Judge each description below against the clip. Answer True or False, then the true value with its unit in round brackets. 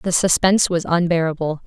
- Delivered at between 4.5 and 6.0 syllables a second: True (5.7 syllables/s)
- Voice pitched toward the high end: False (170 Hz)